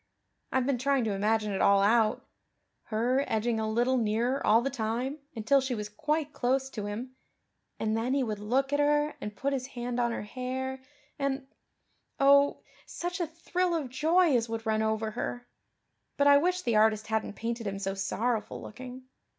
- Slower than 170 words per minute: No, average, 185 wpm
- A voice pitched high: Yes, high, 245 Hz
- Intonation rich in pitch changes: No, average, 3.9 semitones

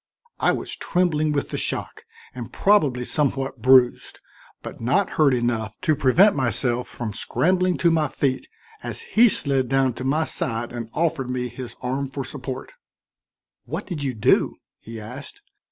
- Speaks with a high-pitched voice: No, low, 135 Hz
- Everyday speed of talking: Yes, average, 160 wpm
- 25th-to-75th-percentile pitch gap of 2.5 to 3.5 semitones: No, average, 3.9 semitones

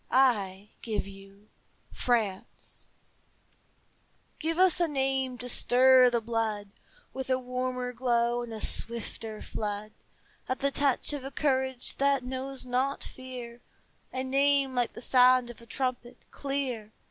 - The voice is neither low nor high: No, very high, 250 Hz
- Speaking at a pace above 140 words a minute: No, slow, 135 wpm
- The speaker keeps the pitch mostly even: Yes, narrow, 2.2 semitones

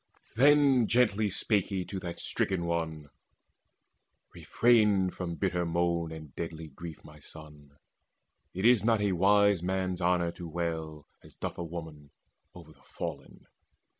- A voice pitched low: Yes, very low, 85 Hz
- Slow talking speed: No, average, 145 wpm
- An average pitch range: Yes, average, 3.8 semitones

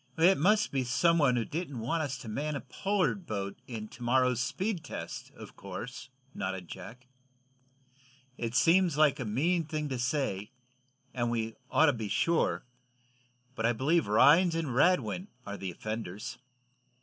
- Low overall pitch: Yes, low, 130 Hz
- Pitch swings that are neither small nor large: No, wide, 6.4 semitones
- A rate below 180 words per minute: Yes, average, 160 wpm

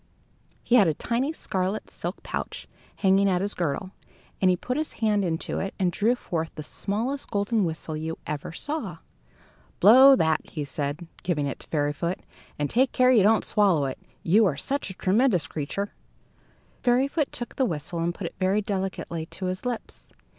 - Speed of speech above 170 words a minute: Yes, average, 185 wpm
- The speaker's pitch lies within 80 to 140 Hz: No, high, 190 Hz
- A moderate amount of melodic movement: No, wide, 6.1 semitones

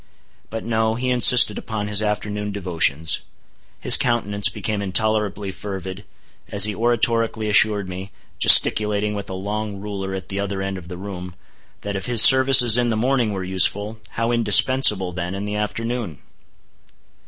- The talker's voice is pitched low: Yes, low, 105 Hz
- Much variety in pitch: No, narrow, 2.6 semitones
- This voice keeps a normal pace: Yes, average, 150 wpm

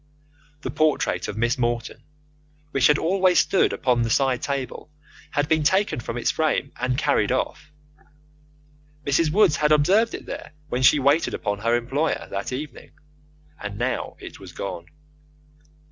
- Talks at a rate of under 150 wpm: No, average, 155 wpm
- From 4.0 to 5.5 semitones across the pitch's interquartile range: Yes, average, 4.5 semitones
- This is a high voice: No, medium, 140 Hz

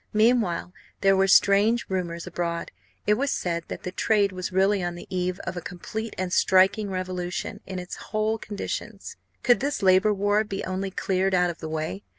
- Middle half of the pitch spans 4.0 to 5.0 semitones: No, narrow, 2.6 semitones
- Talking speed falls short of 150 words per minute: No, average, 185 wpm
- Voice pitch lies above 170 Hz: Yes, high, 190 Hz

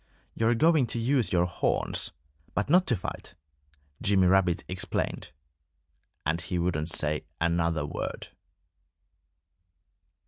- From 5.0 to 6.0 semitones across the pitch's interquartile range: Yes, wide, 5.4 semitones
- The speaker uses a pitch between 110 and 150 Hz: No, very low, 90 Hz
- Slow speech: Yes, slow, 110 wpm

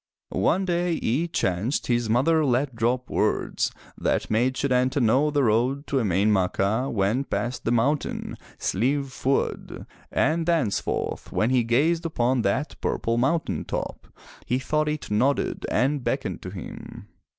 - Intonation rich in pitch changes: No, average, 4.1 semitones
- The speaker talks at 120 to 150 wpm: Yes, average, 145 wpm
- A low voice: Yes, low, 130 Hz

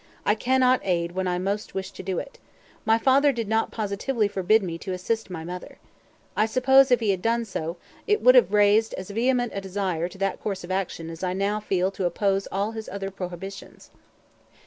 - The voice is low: No, high, 200 Hz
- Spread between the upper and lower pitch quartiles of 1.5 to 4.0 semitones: Yes, average, 3.4 semitones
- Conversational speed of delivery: No, fast, 210 wpm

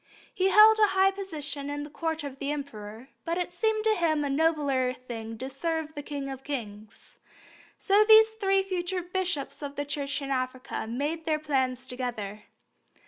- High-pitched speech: Yes, very high, 290 Hz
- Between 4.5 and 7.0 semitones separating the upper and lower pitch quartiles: Yes, average, 5.3 semitones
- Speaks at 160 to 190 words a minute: Yes, average, 180 wpm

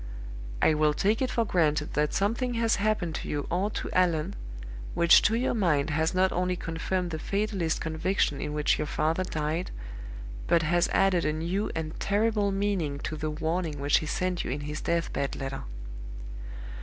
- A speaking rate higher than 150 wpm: Yes, average, 180 wpm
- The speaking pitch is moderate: Yes, medium, 170 Hz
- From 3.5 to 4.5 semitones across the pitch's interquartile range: Yes, average, 4.2 semitones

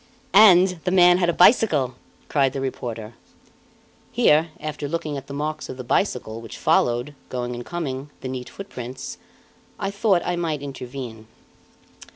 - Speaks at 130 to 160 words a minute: Yes, average, 155 wpm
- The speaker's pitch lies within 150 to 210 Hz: No, medium, 140 Hz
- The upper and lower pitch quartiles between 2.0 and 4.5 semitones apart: No, wide, 5.5 semitones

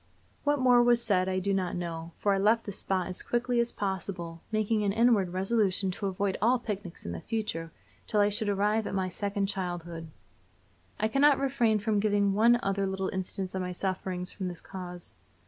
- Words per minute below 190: No, average, 200 wpm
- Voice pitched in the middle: No, high, 195 Hz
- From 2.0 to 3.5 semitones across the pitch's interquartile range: Yes, average, 2.9 semitones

